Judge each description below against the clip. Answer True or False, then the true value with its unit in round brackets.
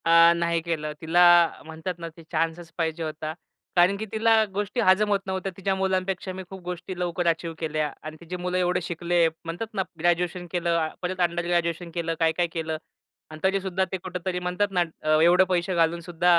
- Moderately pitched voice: True (175 Hz)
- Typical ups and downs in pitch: False (2.0 semitones)